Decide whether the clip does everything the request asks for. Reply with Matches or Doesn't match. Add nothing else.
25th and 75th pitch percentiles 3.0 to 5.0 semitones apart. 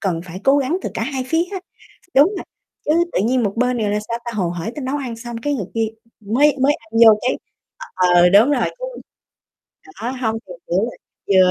Doesn't match